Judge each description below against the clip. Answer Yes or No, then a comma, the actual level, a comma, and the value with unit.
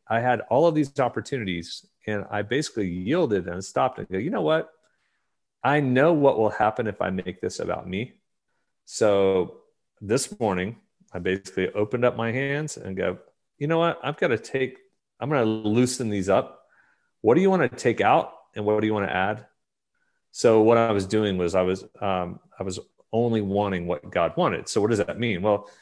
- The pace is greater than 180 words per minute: Yes, fast, 205 wpm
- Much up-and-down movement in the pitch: Yes, wide, 6.1 semitones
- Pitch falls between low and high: No, low, 110 Hz